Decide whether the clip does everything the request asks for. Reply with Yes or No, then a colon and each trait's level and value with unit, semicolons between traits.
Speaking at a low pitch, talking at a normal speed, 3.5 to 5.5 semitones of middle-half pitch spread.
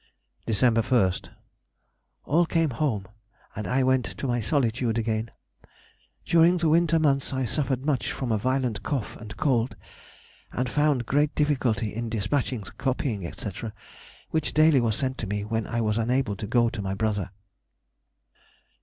Yes: low, 125 Hz; average, 155 wpm; average, 4.2 semitones